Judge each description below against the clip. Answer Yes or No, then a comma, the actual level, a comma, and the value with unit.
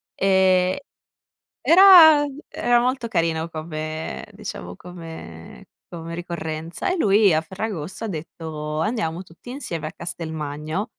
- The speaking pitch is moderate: Yes, medium, 170 Hz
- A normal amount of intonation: Yes, average, 5.0 semitones